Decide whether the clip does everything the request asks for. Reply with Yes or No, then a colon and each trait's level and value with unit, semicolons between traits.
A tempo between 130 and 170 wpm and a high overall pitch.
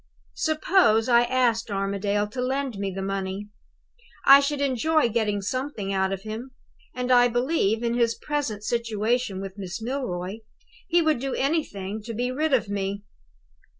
Yes: average, 155 wpm; high, 230 Hz